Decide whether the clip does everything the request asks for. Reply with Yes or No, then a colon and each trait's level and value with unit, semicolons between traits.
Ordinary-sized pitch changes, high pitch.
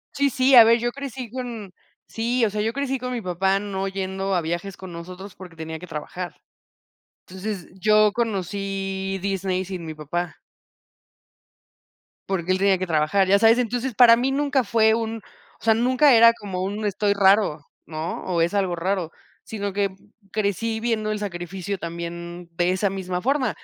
Yes: average, 3.7 semitones; high, 195 Hz